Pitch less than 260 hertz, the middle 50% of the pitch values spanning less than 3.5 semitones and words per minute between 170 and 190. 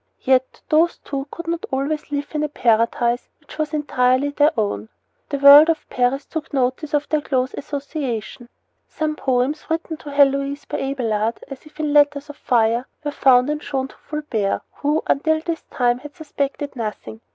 No: very high, 280 Hz; average, 3.1 semitones; average, 175 wpm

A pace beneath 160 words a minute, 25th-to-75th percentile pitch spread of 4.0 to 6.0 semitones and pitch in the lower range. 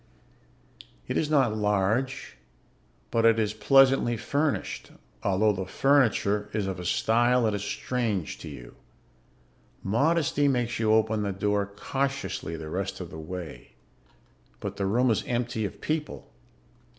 Yes: average, 140 wpm; average, 4.7 semitones; low, 110 Hz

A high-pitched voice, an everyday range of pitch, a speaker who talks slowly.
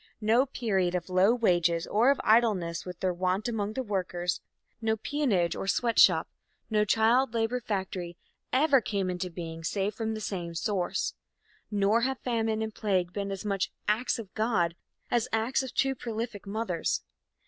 No: high, 210 Hz; average, 4.1 semitones; average, 165 wpm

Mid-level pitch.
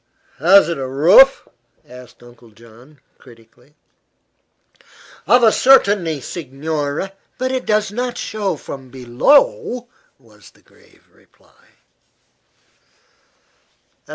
Yes: medium, 155 Hz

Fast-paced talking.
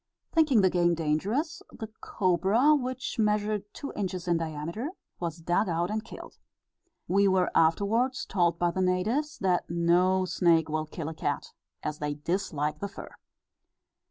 No: average, 155 wpm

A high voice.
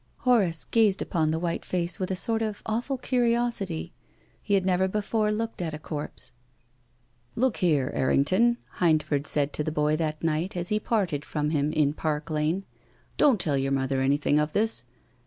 No: medium, 170 Hz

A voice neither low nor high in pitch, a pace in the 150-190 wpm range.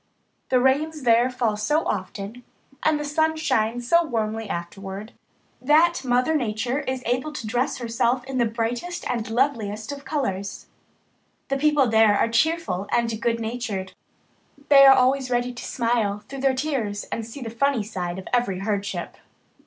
No: high, 240 Hz; average, 160 wpm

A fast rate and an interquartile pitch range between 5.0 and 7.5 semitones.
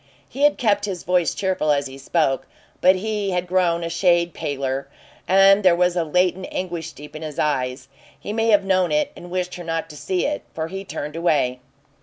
No: fast, 210 wpm; average, 3.7 semitones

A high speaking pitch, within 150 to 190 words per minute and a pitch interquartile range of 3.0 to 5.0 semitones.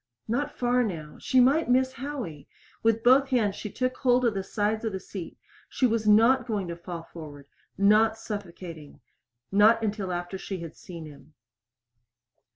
No: high, 210 Hz; average, 165 wpm; wide, 5.6 semitones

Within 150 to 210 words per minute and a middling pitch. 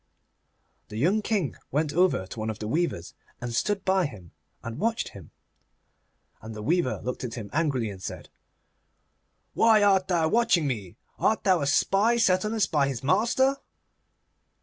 Yes: average, 170 wpm; medium, 160 Hz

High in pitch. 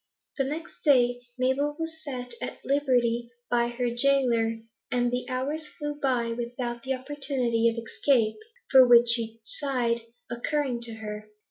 Yes: high, 245 Hz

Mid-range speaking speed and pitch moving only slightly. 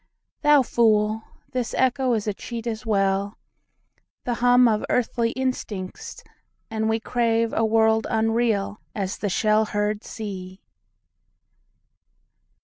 No: slow, 110 wpm; narrow, 2.1 semitones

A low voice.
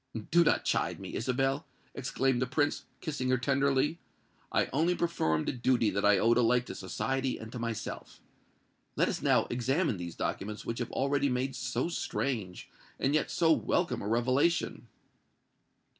Yes: low, 130 Hz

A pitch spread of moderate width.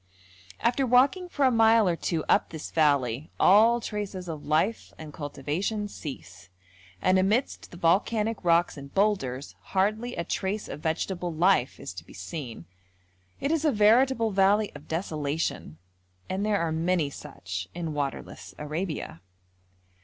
No: wide, 6.3 semitones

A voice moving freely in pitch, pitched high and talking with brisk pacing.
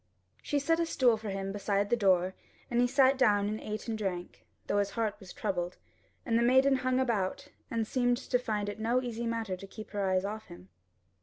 No: average, 3.8 semitones; high, 220 Hz; fast, 220 wpm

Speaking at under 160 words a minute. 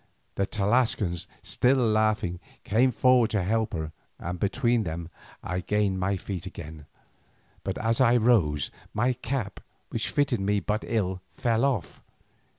Yes: average, 145 wpm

